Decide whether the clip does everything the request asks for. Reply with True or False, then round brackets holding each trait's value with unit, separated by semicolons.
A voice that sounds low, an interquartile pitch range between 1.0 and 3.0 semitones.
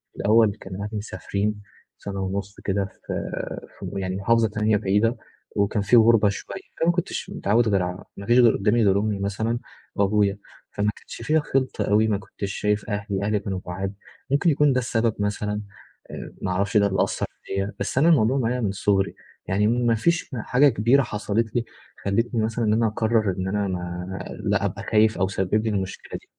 True (105 Hz; 2.7 semitones)